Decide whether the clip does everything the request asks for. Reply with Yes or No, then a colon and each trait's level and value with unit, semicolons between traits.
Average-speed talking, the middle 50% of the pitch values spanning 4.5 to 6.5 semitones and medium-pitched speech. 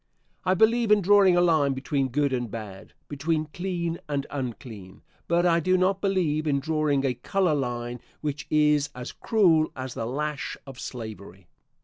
Yes: average, 165 wpm; average, 5.1 semitones; medium, 150 Hz